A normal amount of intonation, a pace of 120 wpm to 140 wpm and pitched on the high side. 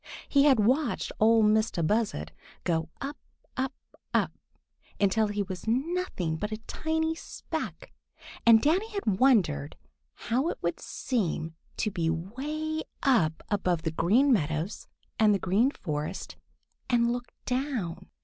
No: wide, 7.2 semitones; slow, 135 wpm; high, 220 Hz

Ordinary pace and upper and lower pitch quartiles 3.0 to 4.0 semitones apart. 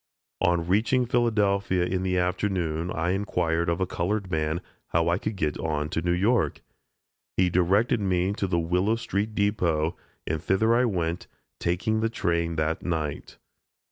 Yes: average, 160 wpm; average, 3.4 semitones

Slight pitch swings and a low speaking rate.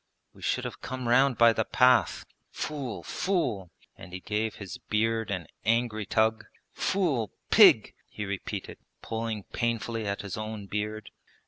No: narrow, 2.2 semitones; average, 145 wpm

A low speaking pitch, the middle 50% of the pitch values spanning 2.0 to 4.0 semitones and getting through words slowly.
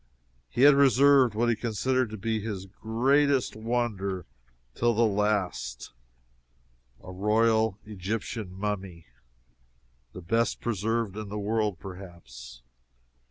Yes: low, 110 Hz; average, 3.4 semitones; slow, 115 wpm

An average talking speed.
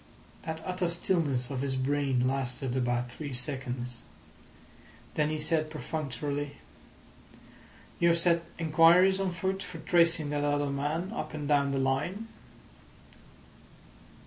No: slow, 125 wpm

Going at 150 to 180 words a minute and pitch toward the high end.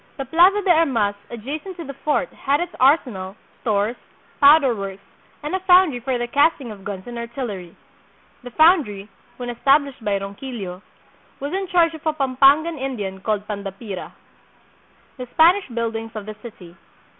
Yes: average, 165 wpm; very high, 250 Hz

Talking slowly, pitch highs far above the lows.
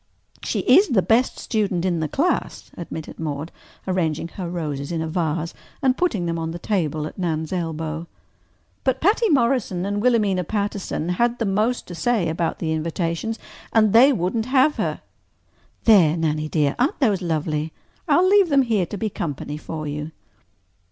No: average, 170 wpm; wide, 6.1 semitones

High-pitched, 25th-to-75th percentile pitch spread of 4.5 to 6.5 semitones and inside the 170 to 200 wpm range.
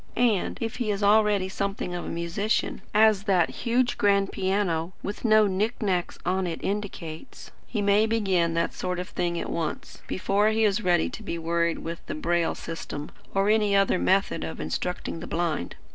No: high, 195 Hz; average, 3.7 semitones; average, 185 wpm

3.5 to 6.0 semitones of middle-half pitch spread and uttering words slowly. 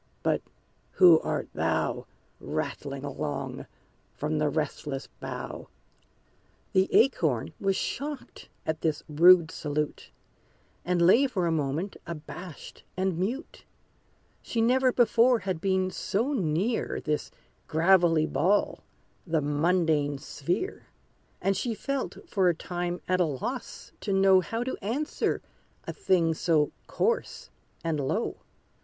Yes: average, 4.7 semitones; slow, 120 wpm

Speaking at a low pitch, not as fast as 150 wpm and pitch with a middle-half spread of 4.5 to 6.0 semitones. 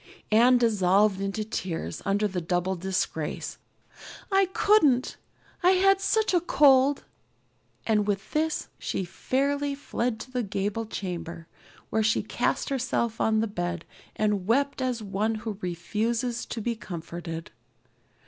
No: high, 220 Hz; slow, 135 wpm; average, 5.2 semitones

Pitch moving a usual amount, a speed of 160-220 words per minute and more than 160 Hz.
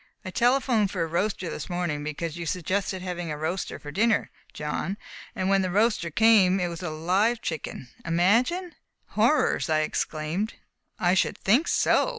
Yes: average, 4.1 semitones; average, 165 wpm; medium, 185 Hz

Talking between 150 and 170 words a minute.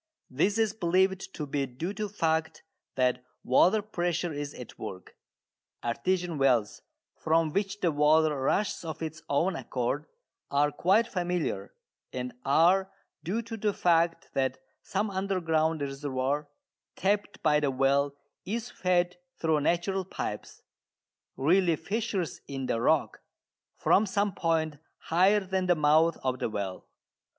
No: average, 140 wpm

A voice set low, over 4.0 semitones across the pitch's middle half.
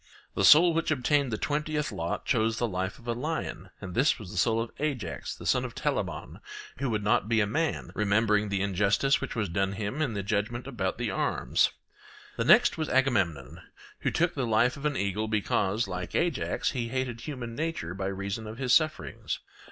Yes: low, 115 Hz; wide, 5.5 semitones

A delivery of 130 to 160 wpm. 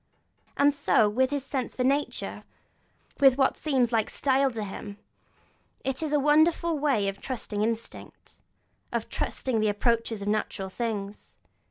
Yes: average, 155 wpm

